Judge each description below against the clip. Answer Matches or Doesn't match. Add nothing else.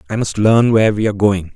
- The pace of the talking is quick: Matches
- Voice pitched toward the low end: Matches